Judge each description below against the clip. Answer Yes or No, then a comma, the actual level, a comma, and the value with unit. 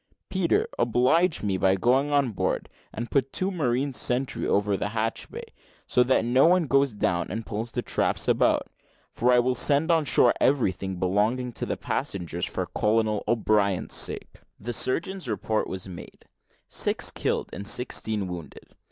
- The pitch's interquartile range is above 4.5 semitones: Yes, average, 4.9 semitones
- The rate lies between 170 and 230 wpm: No, average, 160 wpm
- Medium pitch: No, low, 120 Hz